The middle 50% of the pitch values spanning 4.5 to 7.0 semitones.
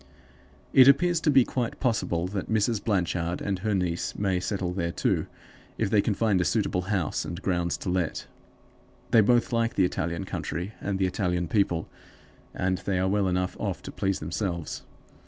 No: average, 3.4 semitones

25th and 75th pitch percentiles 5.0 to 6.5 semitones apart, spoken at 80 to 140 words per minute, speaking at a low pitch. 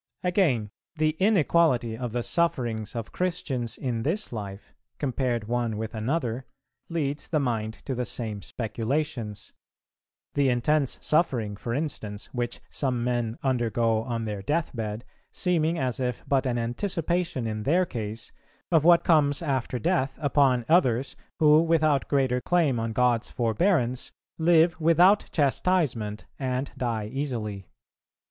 Yes: average, 5.3 semitones; slow, 135 wpm; low, 125 Hz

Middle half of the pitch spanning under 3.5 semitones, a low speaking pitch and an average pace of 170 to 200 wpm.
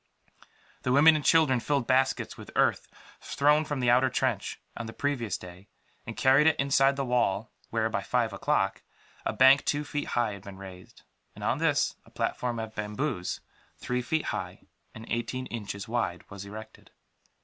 No: average, 4.7 semitones; low, 120 Hz; average, 180 wpm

